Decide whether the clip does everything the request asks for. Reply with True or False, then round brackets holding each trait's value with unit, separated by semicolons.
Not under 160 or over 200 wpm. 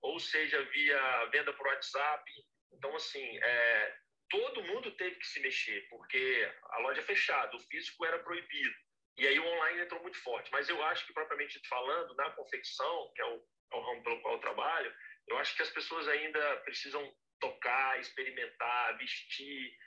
True (180 wpm)